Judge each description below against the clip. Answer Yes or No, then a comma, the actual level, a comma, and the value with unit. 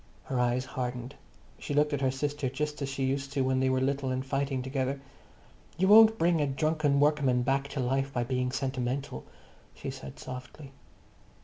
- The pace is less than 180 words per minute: No, average, 185 wpm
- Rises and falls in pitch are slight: Yes, narrow, 1.8 semitones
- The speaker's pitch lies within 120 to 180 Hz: Yes, low, 135 Hz